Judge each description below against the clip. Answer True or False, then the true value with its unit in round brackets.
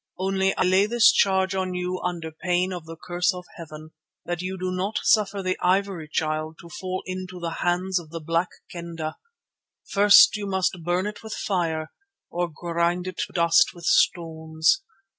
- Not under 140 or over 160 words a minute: False (180 wpm)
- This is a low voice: False (180 Hz)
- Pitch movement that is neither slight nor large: False (2.1 semitones)